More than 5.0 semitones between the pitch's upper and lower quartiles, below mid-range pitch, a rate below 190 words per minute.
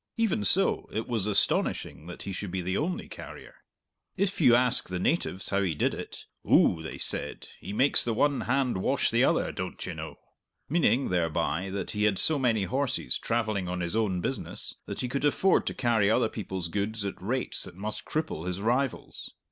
No: wide, 5.5 semitones; low, 105 Hz; average, 195 wpm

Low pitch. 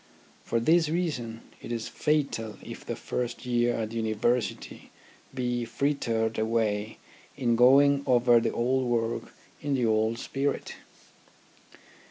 Yes: low, 120 Hz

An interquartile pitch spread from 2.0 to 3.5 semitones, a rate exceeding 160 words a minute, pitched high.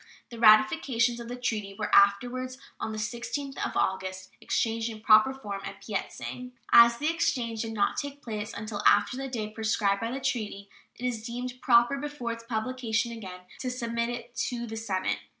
Yes: narrow, 2.6 semitones; average, 185 wpm; high, 230 Hz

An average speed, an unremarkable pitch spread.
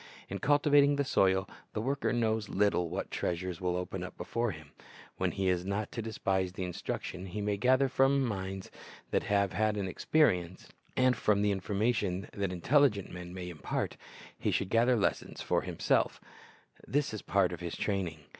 Yes: average, 180 wpm; average, 4.3 semitones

